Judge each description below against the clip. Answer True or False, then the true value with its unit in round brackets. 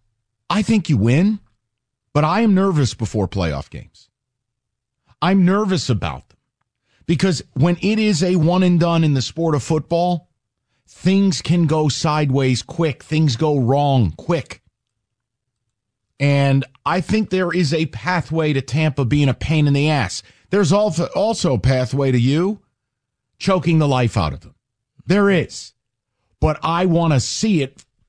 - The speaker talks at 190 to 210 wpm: False (155 wpm)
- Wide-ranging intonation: True (6.5 semitones)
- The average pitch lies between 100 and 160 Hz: True (140 Hz)